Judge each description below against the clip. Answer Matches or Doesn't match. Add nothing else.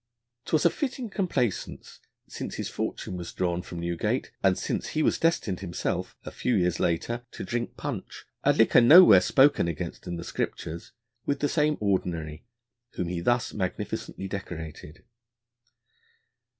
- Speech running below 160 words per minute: Matches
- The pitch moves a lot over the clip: Matches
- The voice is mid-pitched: Doesn't match